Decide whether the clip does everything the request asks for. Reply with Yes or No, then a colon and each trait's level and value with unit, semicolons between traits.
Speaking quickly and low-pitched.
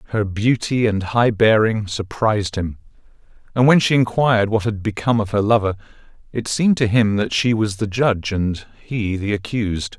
No: average, 180 wpm; low, 110 Hz